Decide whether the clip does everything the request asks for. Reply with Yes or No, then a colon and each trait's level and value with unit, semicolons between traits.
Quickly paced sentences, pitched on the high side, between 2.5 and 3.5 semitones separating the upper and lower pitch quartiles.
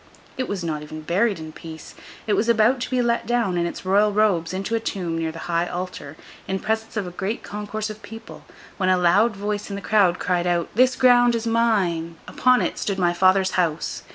No: fast, 220 wpm; high, 195 Hz; average, 4.3 semitones